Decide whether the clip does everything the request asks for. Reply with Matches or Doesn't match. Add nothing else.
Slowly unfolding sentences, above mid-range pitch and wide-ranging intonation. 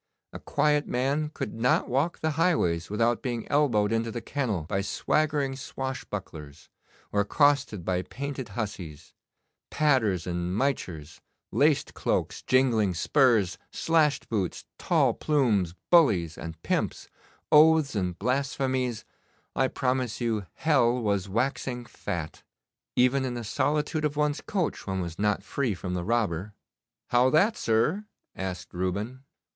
Doesn't match